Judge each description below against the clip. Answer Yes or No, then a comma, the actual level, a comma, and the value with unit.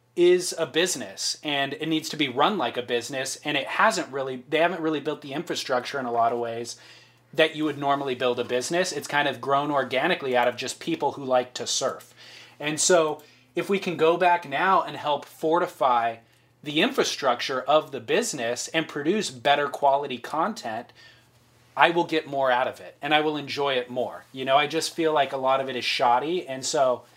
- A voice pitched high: No, medium, 140 Hz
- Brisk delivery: Yes, fast, 210 wpm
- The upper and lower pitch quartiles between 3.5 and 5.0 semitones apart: Yes, average, 4.1 semitones